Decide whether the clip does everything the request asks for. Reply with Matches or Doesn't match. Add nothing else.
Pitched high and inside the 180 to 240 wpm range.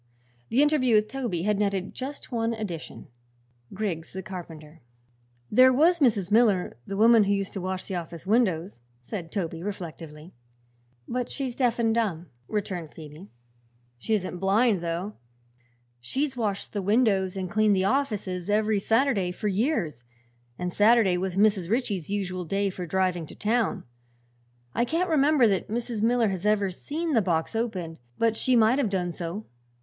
Doesn't match